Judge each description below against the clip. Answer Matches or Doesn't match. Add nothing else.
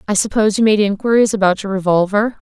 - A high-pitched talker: Matches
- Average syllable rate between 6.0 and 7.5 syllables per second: Matches